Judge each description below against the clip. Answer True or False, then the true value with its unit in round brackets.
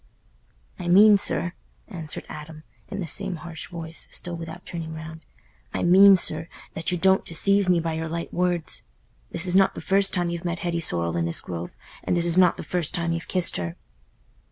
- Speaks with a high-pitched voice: False (170 Hz)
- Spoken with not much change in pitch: True (2.1 semitones)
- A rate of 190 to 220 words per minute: True (195 wpm)